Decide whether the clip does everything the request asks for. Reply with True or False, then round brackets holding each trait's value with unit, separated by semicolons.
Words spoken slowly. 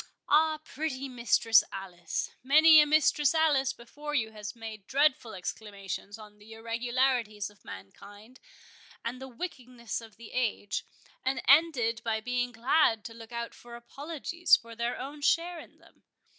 False (150 wpm)